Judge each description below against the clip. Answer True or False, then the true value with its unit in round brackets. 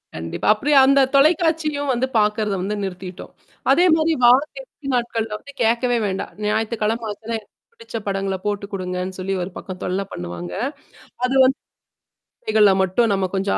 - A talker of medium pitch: False (215 Hz)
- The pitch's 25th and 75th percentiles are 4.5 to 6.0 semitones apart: True (5.2 semitones)